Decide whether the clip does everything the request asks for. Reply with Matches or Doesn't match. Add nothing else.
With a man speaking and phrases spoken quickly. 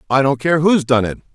Matches